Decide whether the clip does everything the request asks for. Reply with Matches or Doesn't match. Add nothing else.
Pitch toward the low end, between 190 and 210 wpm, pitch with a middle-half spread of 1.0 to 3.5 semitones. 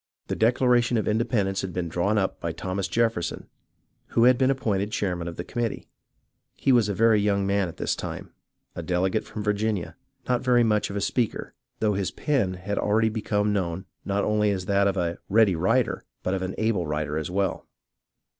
Matches